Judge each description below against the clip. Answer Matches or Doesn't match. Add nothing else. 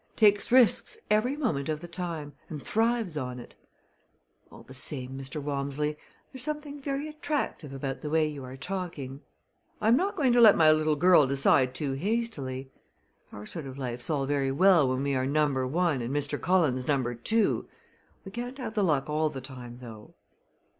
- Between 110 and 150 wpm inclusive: Doesn't match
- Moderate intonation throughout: Doesn't match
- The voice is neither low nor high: Matches